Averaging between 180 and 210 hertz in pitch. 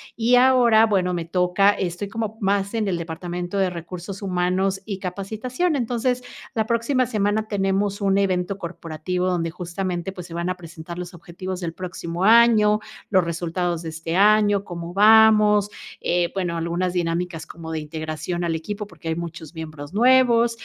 Yes: medium, 185 Hz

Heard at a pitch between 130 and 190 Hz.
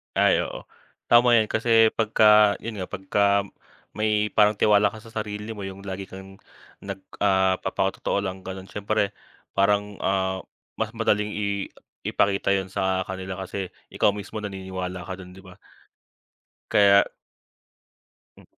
No: low, 100 Hz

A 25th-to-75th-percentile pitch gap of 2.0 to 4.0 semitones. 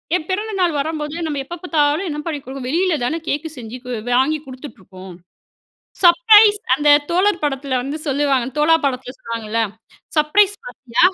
No: average, 4.9 semitones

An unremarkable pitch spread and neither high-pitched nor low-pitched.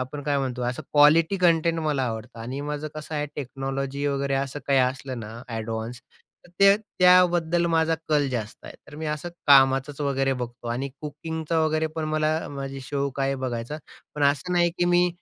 Yes: average, 3.2 semitones; medium, 145 Hz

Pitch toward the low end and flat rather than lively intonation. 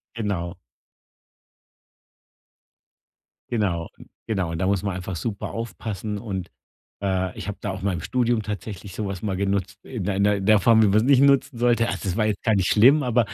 No: low, 100 Hz; average, 3.2 semitones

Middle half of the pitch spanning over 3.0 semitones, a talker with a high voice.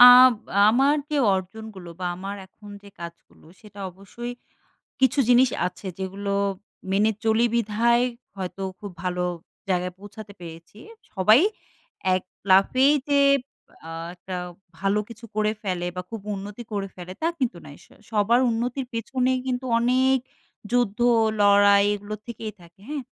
Yes: average, 3.9 semitones; high, 210 Hz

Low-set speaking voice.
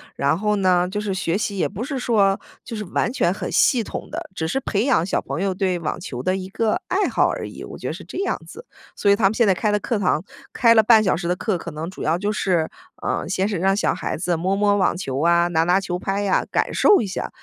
No: high, 195 Hz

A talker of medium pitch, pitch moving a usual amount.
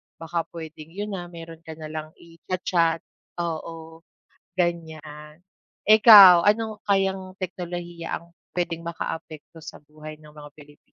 No: medium, 165 Hz; narrow, 2.2 semitones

